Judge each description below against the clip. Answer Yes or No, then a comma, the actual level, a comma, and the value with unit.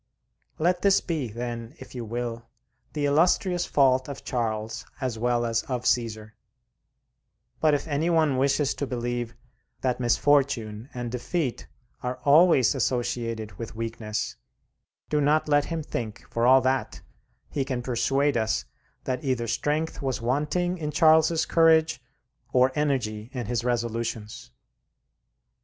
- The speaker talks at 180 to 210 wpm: No, slow, 135 wpm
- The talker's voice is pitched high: No, low, 125 Hz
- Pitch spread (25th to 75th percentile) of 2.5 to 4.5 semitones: Yes, average, 4.0 semitones